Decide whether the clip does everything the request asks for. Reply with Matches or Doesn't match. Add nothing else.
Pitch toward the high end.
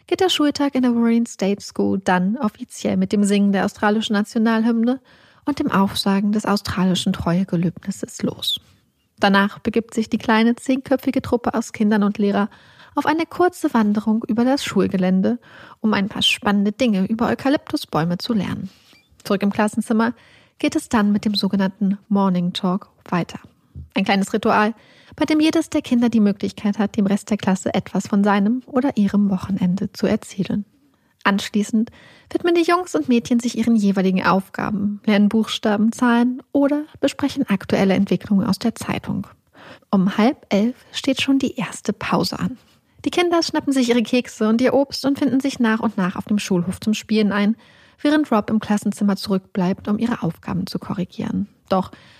Matches